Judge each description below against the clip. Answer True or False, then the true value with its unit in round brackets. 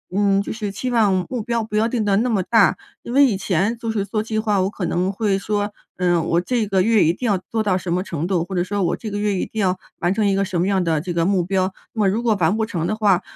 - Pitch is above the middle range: True (200 Hz)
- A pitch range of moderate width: True (3.0 semitones)